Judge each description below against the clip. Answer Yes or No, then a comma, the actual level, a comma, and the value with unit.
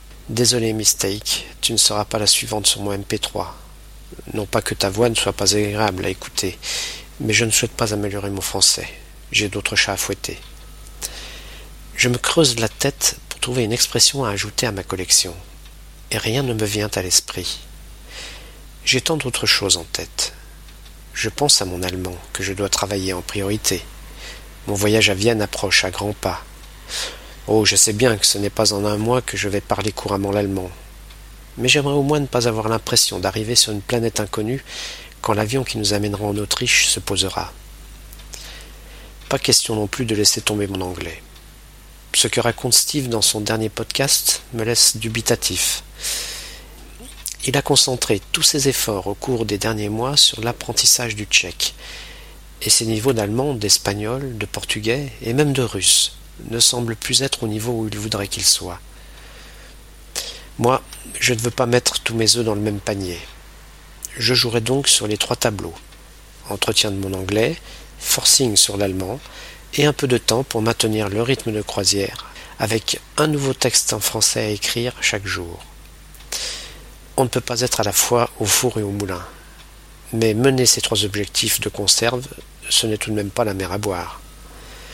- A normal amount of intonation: Yes, average, 3.3 semitones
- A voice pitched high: No, low, 110 Hz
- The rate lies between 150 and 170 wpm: No, average, 180 wpm